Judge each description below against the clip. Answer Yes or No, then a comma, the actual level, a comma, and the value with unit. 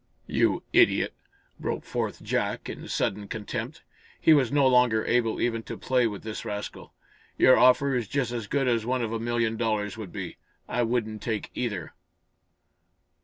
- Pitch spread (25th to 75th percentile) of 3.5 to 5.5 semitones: No, narrow, 2.4 semitones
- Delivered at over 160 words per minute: Yes, average, 170 wpm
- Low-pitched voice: Yes, low, 115 Hz